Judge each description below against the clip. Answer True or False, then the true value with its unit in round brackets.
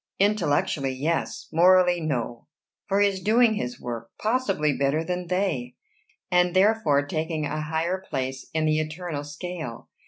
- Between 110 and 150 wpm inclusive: True (145 wpm)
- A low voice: False (160 Hz)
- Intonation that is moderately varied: True (4.4 semitones)